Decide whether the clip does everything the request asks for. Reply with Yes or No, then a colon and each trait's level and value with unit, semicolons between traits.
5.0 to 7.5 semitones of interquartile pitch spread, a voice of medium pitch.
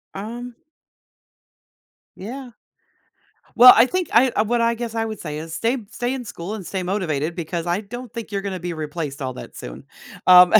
No: wide, 5.6 semitones; high, 200 Hz